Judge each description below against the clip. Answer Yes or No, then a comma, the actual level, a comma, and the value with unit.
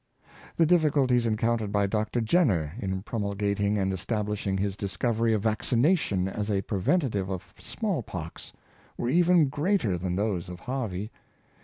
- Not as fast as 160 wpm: Yes, average, 145 wpm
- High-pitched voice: No, low, 105 Hz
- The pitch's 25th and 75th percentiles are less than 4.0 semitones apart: No, average, 4.5 semitones